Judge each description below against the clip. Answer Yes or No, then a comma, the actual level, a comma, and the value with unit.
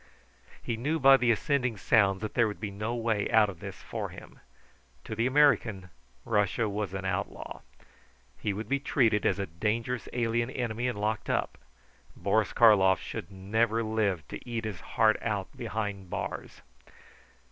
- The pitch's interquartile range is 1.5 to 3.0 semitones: Yes, average, 2.7 semitones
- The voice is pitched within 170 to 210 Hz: No, low, 110 Hz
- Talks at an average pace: Yes, average, 165 wpm